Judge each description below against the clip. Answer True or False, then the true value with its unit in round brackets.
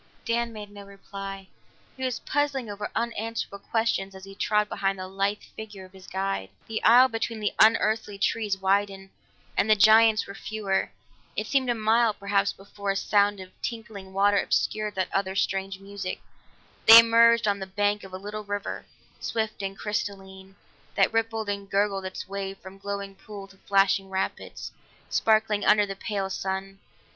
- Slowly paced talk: False (170 wpm)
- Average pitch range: False (1.9 semitones)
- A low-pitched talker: False (200 Hz)